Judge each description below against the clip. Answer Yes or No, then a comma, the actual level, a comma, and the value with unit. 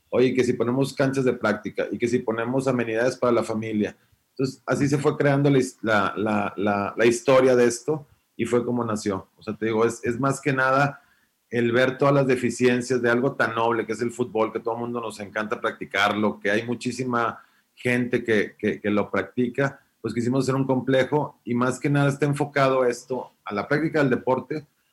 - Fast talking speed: Yes, fast, 205 wpm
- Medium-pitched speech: No, low, 125 Hz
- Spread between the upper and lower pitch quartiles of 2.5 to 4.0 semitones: Yes, average, 2.8 semitones